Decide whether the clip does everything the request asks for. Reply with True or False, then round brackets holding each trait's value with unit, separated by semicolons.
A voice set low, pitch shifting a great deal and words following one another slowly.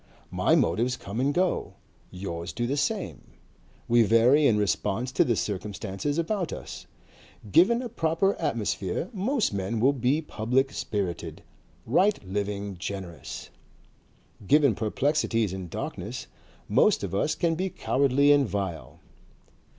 True (120 Hz; 7.0 semitones; 130 wpm)